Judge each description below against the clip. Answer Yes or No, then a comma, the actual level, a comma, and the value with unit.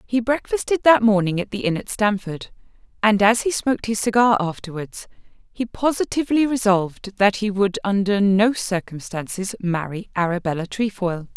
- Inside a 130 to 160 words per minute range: Yes, average, 150 wpm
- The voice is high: Yes, high, 205 Hz